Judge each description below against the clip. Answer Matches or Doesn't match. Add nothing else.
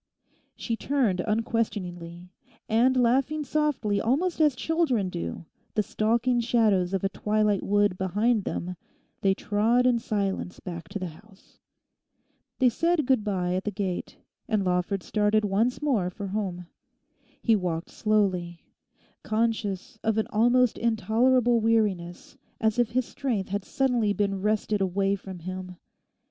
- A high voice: Matches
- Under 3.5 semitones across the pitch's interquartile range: Doesn't match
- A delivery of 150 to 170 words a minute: Doesn't match